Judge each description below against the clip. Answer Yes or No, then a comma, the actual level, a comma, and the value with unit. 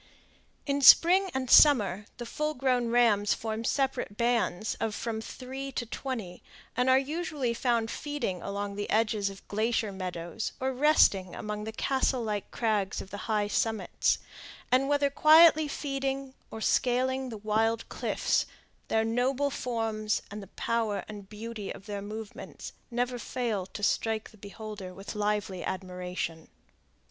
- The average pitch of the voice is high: Yes, high, 225 Hz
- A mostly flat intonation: No, average, 4.1 semitones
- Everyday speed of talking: Yes, average, 150 wpm